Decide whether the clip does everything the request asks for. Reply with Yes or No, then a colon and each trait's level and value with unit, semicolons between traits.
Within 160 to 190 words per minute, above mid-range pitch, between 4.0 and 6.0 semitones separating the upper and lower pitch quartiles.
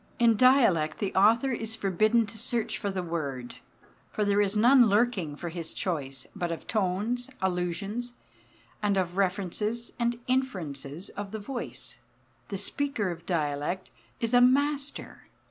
No: average, 145 wpm; high, 205 Hz; average, 5.2 semitones